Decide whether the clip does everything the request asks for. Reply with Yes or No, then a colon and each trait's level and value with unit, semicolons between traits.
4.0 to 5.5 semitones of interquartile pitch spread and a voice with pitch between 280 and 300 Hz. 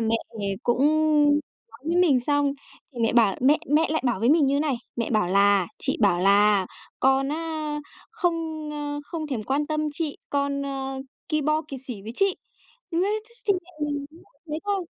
Yes: average, 5.0 semitones; very high, 285 Hz